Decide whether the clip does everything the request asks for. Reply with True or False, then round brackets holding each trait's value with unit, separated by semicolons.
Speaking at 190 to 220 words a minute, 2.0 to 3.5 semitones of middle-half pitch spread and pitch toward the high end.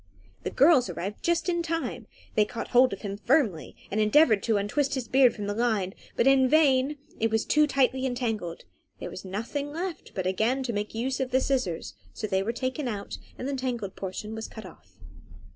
False (205 wpm; 4.7 semitones; 240 Hz)